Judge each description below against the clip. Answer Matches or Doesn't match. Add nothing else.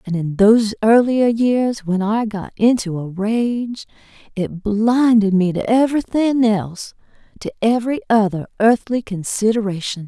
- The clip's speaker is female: Matches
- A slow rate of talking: Matches